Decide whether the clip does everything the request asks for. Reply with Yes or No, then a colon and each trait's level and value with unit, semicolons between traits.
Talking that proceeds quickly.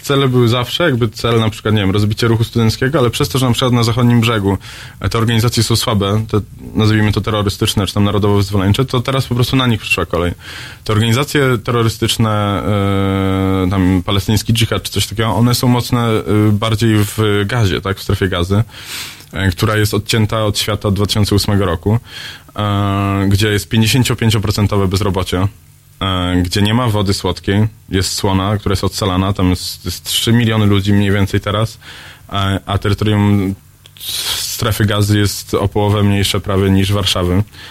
Yes: fast, 165 wpm